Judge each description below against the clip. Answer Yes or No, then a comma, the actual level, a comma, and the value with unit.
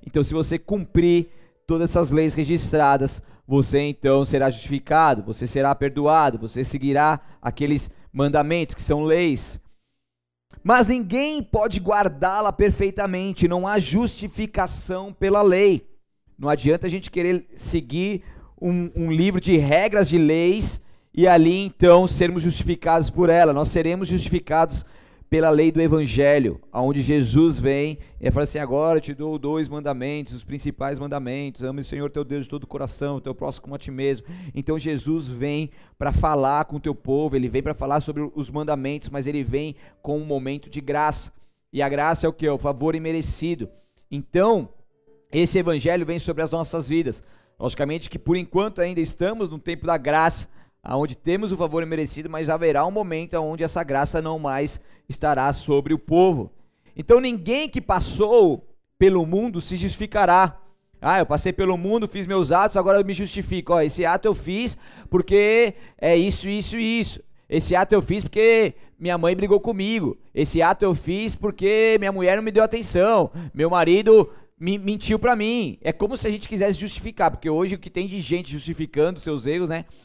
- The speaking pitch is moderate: Yes, medium, 165 Hz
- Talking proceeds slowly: No, average, 175 wpm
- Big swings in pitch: No, average, 4.4 semitones